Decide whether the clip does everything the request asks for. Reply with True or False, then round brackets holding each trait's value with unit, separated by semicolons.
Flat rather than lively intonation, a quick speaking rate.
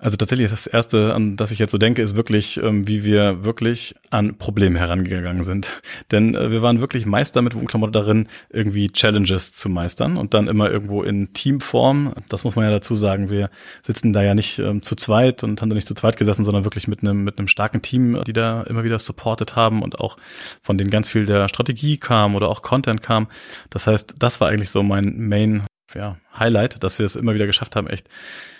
True (2.0 semitones; 215 wpm)